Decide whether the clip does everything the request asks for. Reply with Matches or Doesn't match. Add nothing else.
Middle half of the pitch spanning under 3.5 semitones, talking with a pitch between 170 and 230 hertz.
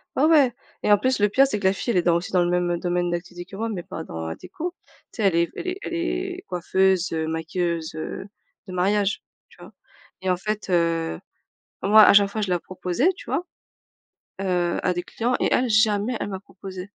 Doesn't match